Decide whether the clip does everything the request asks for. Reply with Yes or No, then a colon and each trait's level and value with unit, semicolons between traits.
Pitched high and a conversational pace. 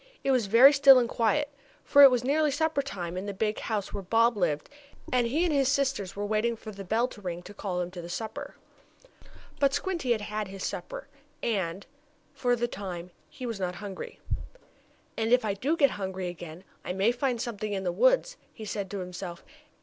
No: high, 215 Hz; fast, 210 wpm